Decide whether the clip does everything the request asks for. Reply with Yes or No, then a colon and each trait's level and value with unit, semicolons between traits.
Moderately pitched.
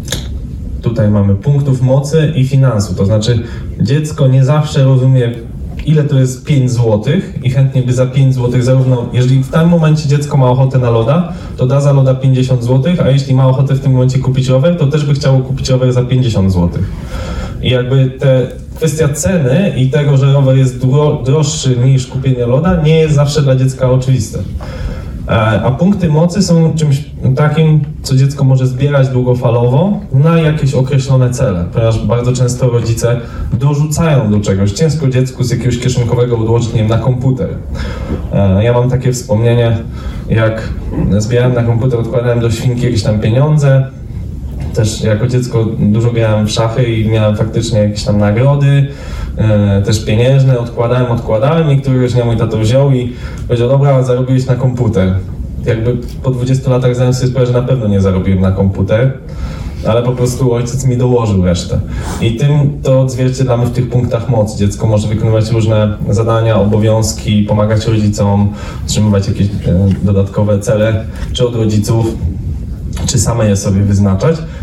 No: low, 125 Hz